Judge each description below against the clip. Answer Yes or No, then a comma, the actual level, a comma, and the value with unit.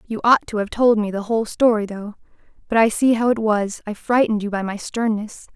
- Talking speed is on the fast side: Yes, fast, 225 wpm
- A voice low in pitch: No, high, 220 Hz